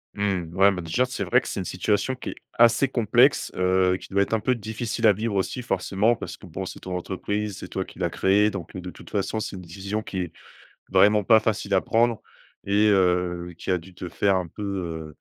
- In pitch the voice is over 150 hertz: No, very low, 95 Hz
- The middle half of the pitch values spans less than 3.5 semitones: Yes, average, 2.7 semitones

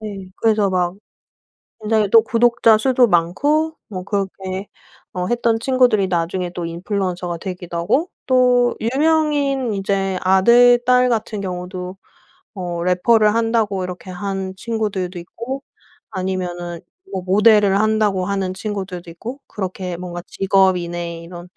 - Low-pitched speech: No, high, 195 Hz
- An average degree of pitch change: Yes, average, 4.0 semitones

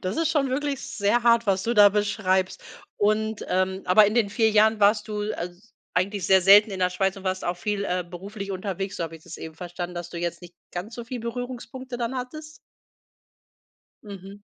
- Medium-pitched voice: No, high, 200 Hz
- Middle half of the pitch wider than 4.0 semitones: No, average, 3.6 semitones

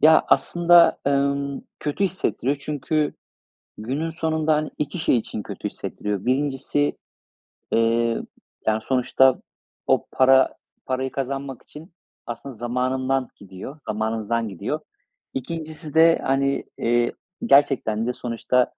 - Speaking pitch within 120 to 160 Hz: Yes, low, 135 Hz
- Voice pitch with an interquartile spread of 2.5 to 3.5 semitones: No, average, 4.0 semitones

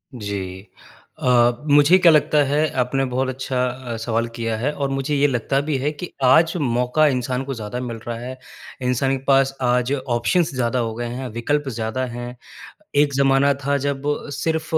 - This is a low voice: Yes, low, 130 Hz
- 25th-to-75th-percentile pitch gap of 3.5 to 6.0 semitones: No, average, 2.8 semitones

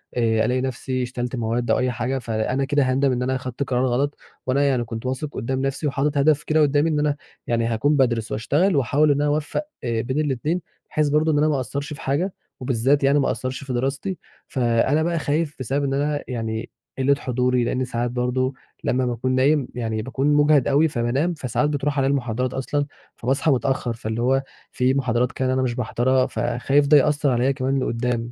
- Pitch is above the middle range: No, low, 130 Hz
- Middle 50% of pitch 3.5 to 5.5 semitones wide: No, average, 2.8 semitones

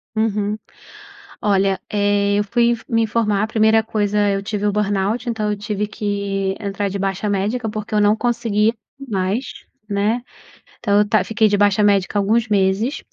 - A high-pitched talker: Yes, high, 210 Hz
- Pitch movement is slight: Yes, narrow, 1.6 semitones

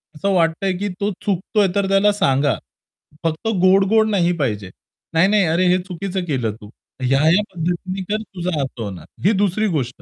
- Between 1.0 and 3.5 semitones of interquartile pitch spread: No, average, 4.1 semitones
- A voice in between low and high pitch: Yes, medium, 180 Hz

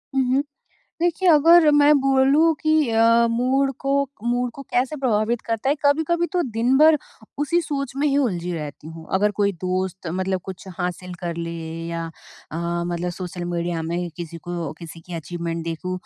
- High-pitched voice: Yes, high, 210 Hz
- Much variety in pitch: Yes, wide, 8.1 semitones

